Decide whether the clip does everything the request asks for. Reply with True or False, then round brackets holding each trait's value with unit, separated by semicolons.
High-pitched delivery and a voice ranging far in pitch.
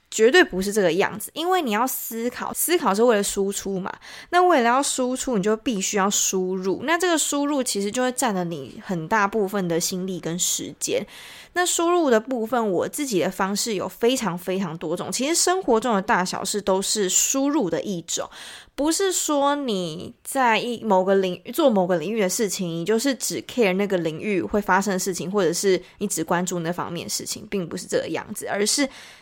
True (210 Hz; 5.8 semitones)